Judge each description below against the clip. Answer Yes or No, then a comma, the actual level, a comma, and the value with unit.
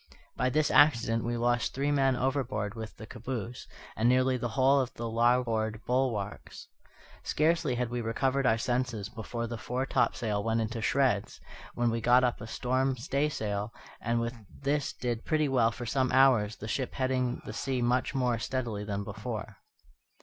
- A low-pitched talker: Yes, low, 120 Hz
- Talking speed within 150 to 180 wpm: Yes, average, 170 wpm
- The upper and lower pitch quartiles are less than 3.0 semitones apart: Yes, narrow, 2.6 semitones